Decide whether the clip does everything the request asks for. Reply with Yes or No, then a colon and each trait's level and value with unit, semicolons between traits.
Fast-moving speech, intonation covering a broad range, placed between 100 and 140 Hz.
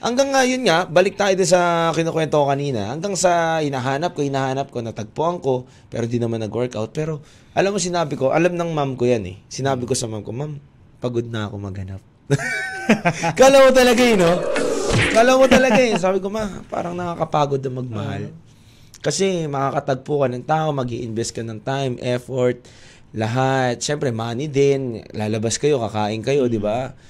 Yes: fast, 180 wpm; wide, 6.0 semitones; low, 135 Hz